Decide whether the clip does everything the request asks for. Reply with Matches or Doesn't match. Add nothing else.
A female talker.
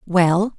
Matches